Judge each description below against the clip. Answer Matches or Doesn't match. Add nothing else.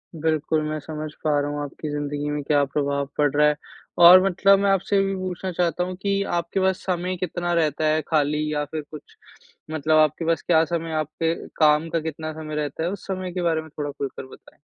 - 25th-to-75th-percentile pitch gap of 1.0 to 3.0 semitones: Matches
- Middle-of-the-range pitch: Matches